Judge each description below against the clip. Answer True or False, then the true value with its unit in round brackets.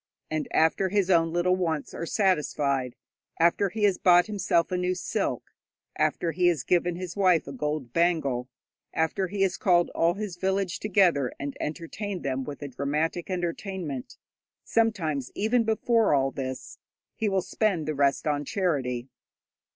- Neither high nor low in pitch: True (175 Hz)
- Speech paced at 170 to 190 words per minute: False (160 wpm)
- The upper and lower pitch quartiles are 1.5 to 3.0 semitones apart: False (4.6 semitones)